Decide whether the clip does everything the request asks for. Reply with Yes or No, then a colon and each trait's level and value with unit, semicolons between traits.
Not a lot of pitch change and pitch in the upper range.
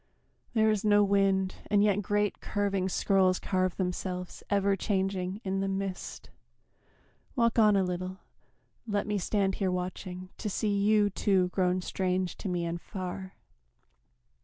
Yes: narrow, 1.8 semitones; high, 195 Hz